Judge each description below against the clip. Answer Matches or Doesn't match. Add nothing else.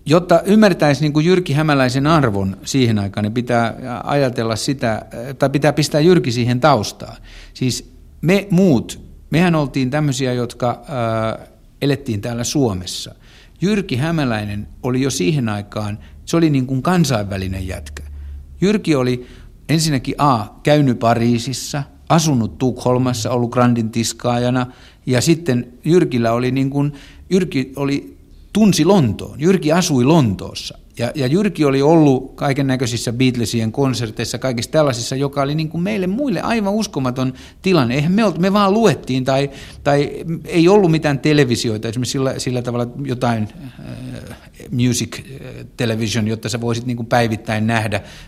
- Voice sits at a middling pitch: Doesn't match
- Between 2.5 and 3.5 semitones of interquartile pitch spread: Doesn't match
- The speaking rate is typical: Matches